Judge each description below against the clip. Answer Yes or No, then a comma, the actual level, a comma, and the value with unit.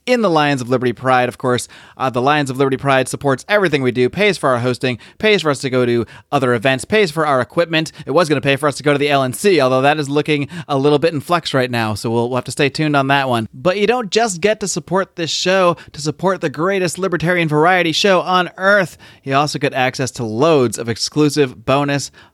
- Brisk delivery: Yes, fast, 255 wpm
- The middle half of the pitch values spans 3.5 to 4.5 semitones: No, average, 5.2 semitones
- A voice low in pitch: No, medium, 145 Hz